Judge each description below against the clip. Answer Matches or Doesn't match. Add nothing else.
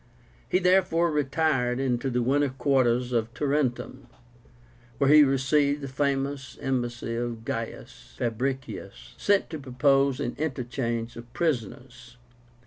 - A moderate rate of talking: Doesn't match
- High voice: Doesn't match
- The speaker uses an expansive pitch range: Doesn't match